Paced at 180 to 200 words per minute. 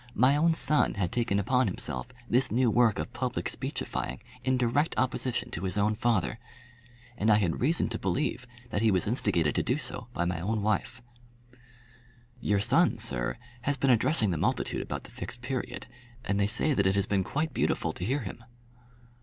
Yes: average, 190 wpm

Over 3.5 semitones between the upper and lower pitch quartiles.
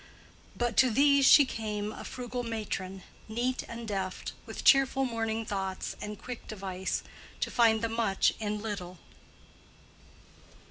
No: average, 3.1 semitones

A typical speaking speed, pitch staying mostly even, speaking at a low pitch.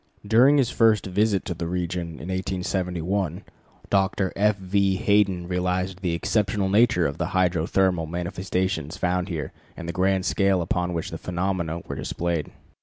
Yes: average, 155 wpm; narrow, 2.1 semitones; very low, 90 Hz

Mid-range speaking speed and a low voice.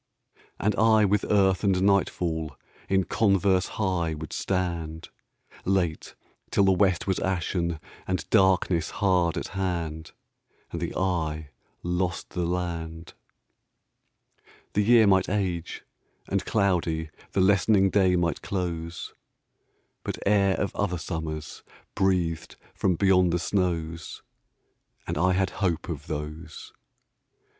No: slow, 120 wpm; very low, 90 Hz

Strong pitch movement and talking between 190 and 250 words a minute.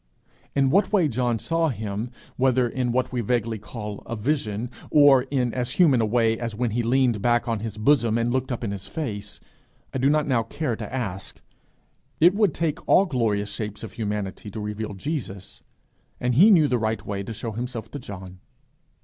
No: average, 3.8 semitones; average, 200 wpm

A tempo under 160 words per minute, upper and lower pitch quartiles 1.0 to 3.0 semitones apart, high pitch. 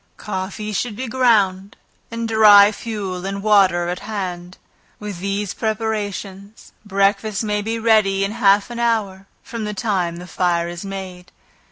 Yes: average, 150 wpm; narrow, 2.4 semitones; high, 200 Hz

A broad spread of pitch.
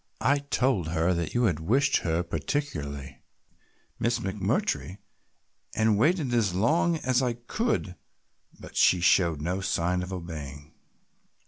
Yes: wide, 7.2 semitones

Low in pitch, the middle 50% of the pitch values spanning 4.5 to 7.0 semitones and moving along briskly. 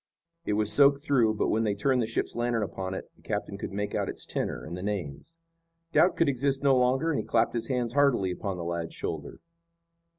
Yes: low, 115 Hz; wide, 5.4 semitones; fast, 225 wpm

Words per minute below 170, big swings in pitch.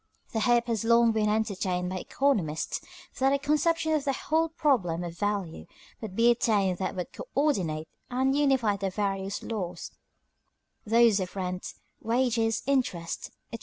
Yes: average, 150 wpm; wide, 5.8 semitones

